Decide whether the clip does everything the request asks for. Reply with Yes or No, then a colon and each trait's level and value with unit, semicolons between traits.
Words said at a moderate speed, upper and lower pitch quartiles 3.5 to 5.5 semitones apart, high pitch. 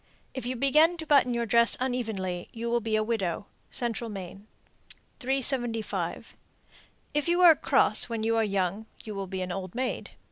Yes: average, 175 wpm; average, 4.2 semitones; high, 230 Hz